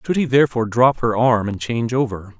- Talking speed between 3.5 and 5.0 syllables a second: No, 6.3 syllables/s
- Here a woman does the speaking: No, male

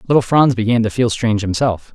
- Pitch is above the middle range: No, low, 115 Hz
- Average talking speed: No, fast, 215 wpm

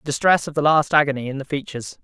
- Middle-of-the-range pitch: Yes, medium, 145 Hz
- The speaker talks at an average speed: No, fast, 265 wpm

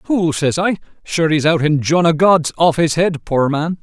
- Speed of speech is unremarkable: No, fast, 235 wpm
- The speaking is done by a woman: No, male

